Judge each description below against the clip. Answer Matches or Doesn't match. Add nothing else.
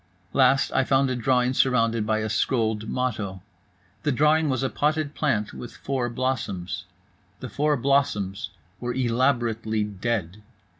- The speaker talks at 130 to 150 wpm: Matches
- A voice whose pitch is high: Doesn't match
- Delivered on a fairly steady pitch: Doesn't match